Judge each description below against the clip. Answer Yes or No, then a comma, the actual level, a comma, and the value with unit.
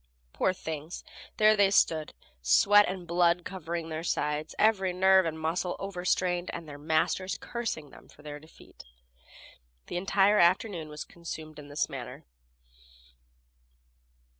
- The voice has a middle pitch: Yes, medium, 175 Hz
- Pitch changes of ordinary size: Yes, average, 3.3 semitones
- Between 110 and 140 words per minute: Yes, slow, 135 wpm